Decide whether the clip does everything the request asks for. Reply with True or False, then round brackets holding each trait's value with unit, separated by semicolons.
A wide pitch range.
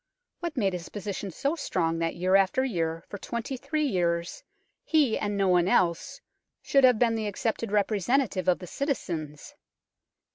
True (6.4 semitones)